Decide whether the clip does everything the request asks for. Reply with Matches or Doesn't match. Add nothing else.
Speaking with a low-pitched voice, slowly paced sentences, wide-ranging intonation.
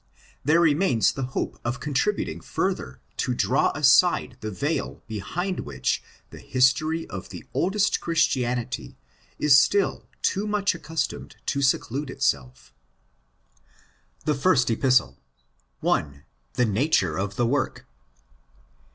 Matches